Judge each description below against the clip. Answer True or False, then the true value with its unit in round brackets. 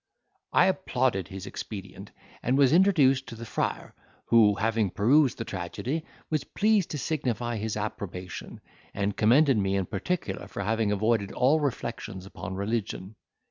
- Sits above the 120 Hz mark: False (115 Hz)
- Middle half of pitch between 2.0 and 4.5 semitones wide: False (5.5 semitones)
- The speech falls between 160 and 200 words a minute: False (145 wpm)